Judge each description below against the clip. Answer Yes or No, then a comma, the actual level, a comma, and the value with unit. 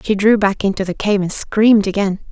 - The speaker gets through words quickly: Yes, fast, 235 wpm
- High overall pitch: Yes, high, 200 Hz